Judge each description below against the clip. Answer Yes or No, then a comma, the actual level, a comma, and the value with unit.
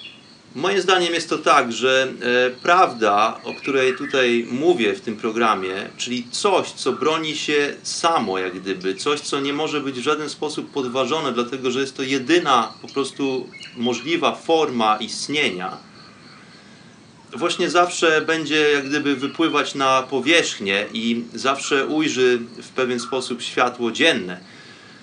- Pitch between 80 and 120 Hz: No, low, 135 Hz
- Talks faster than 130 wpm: Yes, average, 140 wpm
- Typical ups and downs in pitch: Yes, average, 3.8 semitones